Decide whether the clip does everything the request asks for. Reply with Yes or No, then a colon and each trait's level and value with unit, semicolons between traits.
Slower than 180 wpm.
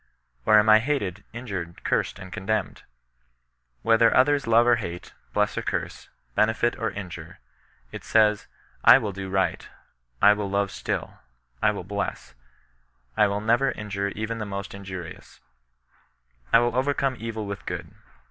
Yes: average, 155 wpm